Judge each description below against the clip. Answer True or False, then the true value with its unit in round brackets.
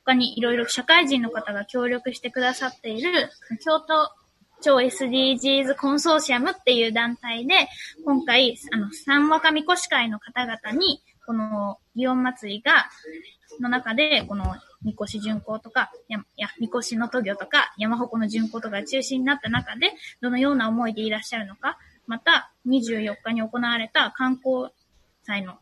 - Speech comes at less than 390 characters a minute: True (295 characters per minute)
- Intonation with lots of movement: False (3.6 semitones)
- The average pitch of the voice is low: False (245 Hz)